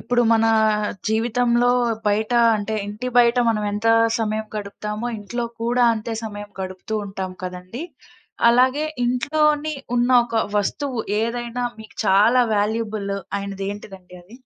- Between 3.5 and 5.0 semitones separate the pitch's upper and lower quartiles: No, average, 2.8 semitones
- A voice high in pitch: Yes, high, 220 Hz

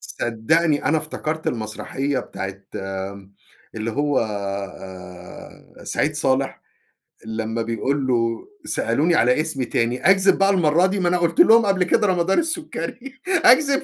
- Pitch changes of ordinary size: No, wide, 8.5 semitones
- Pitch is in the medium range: Yes, medium, 145 Hz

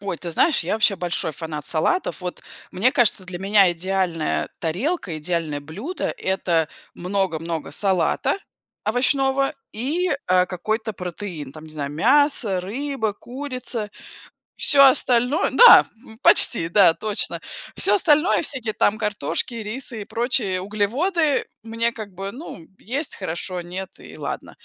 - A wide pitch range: Yes, wide, 6.2 semitones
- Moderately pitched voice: No, high, 205 Hz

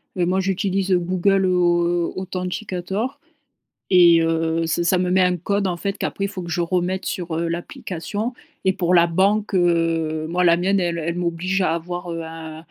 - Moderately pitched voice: Yes, medium, 180 Hz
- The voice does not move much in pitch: Yes, narrow, 2.0 semitones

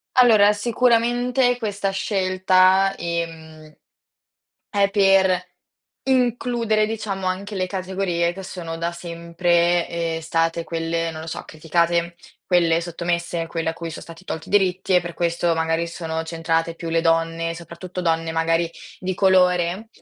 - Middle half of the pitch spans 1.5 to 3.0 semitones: Yes, narrow, 2.6 semitones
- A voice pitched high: No, medium, 175 Hz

